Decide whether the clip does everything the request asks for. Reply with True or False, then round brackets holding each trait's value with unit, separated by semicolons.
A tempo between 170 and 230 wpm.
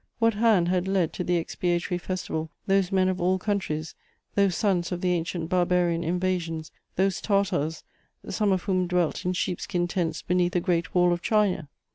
True (180 wpm)